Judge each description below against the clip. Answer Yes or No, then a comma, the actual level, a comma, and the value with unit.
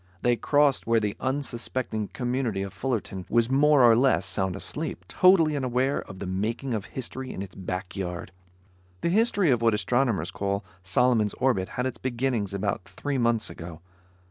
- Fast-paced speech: No, average, 170 wpm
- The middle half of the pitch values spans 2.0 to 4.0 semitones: No, average, 5.1 semitones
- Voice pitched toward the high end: No, low, 115 Hz